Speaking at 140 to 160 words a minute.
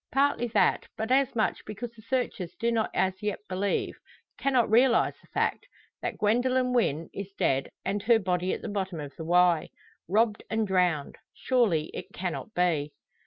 No: average, 170 wpm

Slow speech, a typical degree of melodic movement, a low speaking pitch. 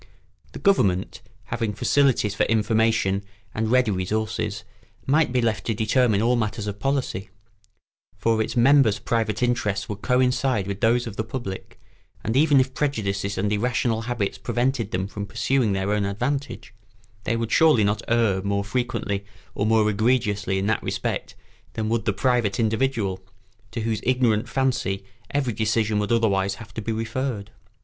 No: average, 160 wpm; average, 3.2 semitones; low, 110 Hz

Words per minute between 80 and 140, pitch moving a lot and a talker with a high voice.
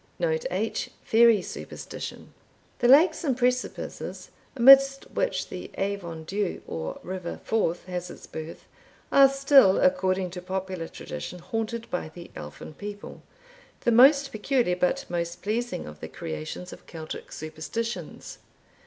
Yes: slow, 135 wpm; wide, 6.4 semitones; high, 200 Hz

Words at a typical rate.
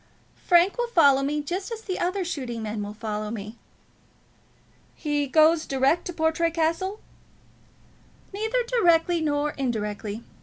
No: slow, 130 wpm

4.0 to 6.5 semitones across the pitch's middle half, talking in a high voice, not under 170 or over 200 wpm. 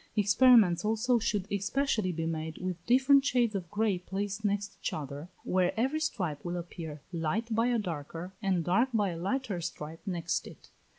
Yes: average, 4.9 semitones; high, 195 Hz; average, 175 wpm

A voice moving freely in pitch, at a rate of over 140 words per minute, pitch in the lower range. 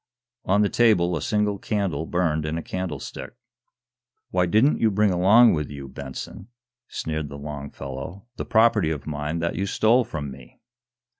Yes: wide, 5.8 semitones; average, 165 wpm; very low, 85 Hz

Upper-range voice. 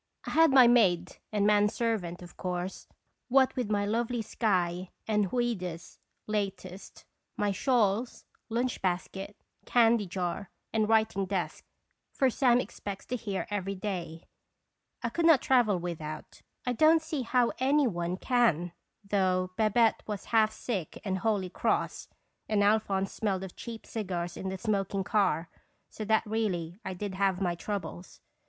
Yes: high, 205 Hz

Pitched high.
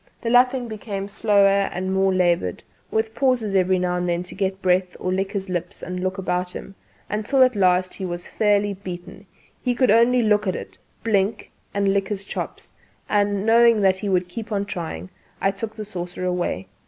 Yes: high, 195 Hz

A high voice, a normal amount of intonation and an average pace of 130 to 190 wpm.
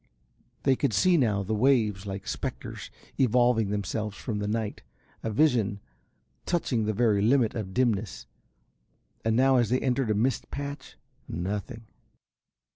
No: low, 110 Hz; average, 3.6 semitones; average, 140 wpm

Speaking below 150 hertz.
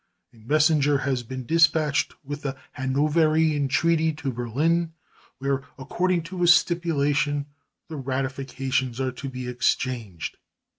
Yes: medium, 140 Hz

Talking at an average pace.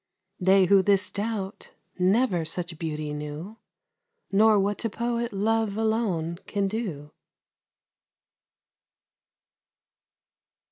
No: slow, 90 wpm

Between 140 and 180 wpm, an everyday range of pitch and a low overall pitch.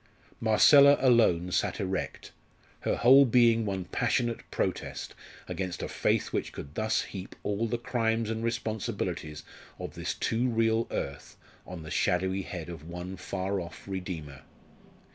Yes: average, 145 wpm; average, 4.3 semitones; low, 100 Hz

